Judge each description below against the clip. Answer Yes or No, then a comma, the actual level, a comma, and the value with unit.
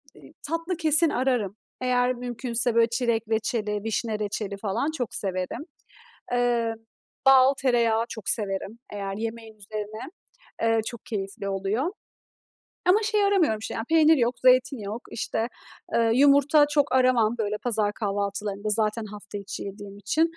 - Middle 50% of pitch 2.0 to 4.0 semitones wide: Yes, average, 3.6 semitones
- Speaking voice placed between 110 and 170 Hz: No, high, 230 Hz